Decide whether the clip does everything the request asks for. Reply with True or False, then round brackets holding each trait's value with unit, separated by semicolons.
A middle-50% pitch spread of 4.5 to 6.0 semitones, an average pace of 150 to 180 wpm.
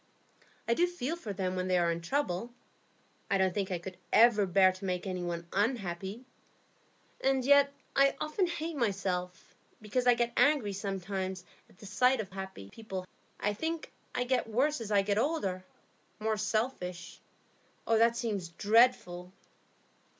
True (5.0 semitones; 160 wpm)